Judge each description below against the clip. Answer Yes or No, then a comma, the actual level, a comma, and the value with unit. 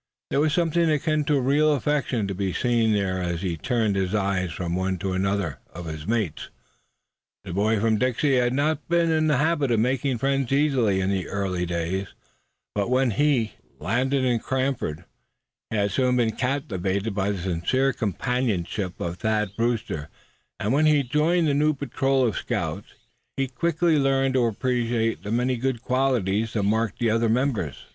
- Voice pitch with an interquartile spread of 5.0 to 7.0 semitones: Yes, wide, 5.6 semitones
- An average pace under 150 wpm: No, average, 175 wpm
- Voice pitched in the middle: No, low, 115 Hz